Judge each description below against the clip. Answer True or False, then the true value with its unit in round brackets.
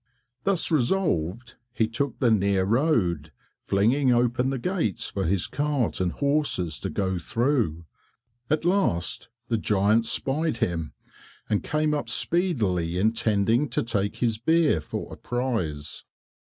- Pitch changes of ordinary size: False (7.0 semitones)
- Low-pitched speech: True (115 Hz)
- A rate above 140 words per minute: False (135 wpm)